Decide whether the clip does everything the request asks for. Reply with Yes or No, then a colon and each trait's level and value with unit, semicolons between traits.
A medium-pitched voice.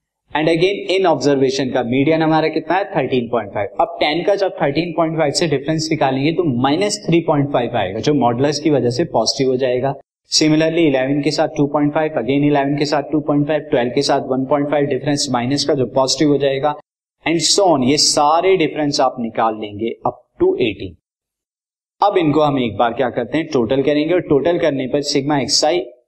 Yes: medium, 145 Hz